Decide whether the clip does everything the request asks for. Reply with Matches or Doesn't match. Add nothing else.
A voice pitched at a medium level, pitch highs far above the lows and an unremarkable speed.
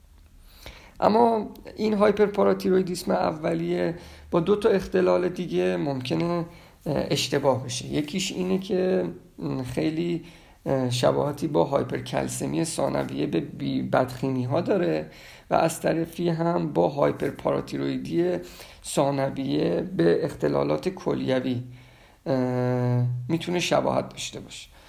Doesn't match